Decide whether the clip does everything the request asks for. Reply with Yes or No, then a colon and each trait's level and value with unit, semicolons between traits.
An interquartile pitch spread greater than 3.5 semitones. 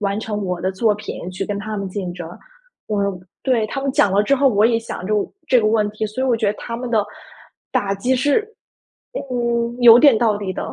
No: average, 3.1 semitones